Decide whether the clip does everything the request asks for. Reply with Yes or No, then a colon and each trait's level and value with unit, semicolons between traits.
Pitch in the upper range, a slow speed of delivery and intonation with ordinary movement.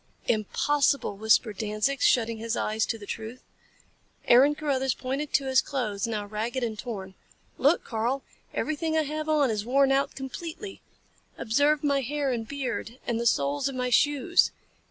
No: very high, 255 Hz; average, 160 wpm; average, 4.4 semitones